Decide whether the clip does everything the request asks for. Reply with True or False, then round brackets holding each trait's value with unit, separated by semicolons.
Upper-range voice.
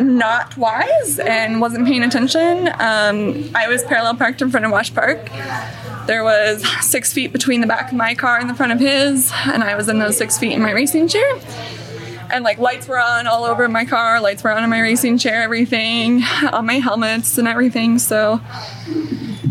True (235 Hz)